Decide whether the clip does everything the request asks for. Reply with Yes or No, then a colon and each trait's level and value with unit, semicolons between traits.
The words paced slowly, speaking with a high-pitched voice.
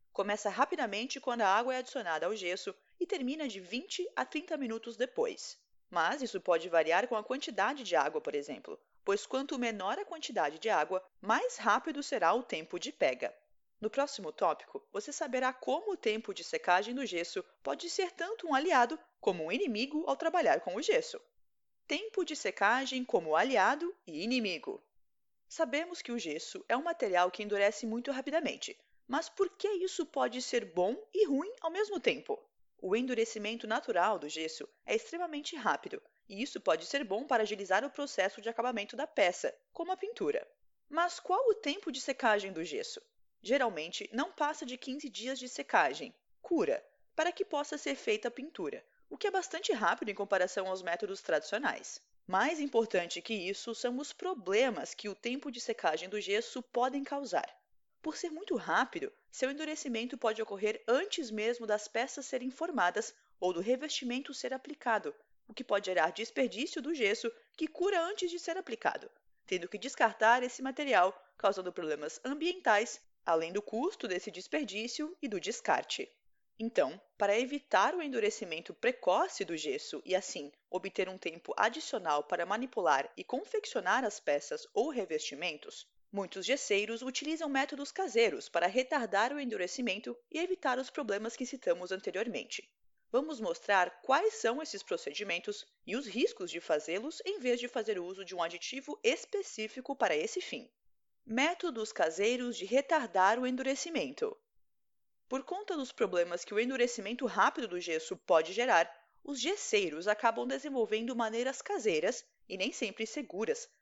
No: average, 160 wpm; very high, 260 Hz